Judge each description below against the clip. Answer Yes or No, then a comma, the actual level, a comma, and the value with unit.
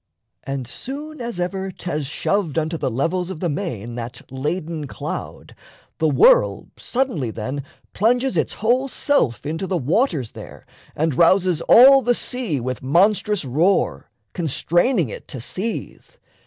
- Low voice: No, medium, 175 Hz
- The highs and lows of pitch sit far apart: Yes, wide, 7.7 semitones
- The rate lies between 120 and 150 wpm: Yes, average, 140 wpm